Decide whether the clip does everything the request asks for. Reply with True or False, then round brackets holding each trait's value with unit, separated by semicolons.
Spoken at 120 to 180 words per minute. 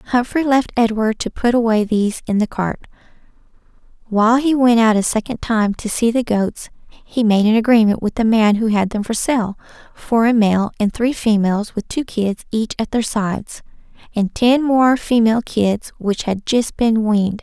False (195 wpm)